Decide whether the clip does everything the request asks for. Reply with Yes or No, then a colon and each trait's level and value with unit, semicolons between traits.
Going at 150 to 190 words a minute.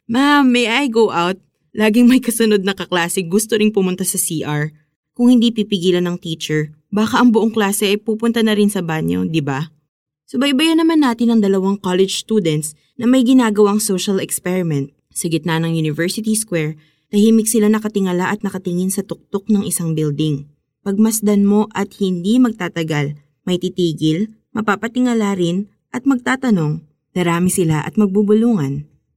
Yes: fast, 155 wpm